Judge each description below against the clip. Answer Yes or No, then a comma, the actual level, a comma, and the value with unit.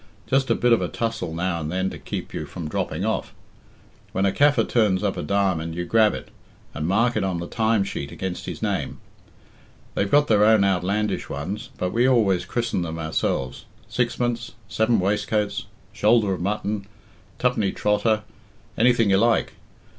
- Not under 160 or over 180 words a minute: Yes, average, 175 wpm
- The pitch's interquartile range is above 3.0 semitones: Yes, average, 3.7 semitones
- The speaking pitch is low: Yes, low, 100 Hz